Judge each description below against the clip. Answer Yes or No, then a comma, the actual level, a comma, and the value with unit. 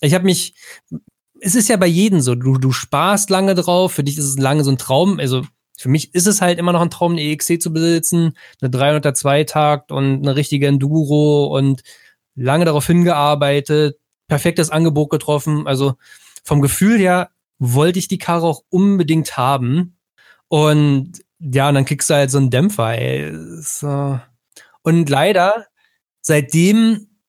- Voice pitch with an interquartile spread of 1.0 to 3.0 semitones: No, average, 3.9 semitones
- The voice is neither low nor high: Yes, medium, 150 Hz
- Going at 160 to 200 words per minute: Yes, average, 165 wpm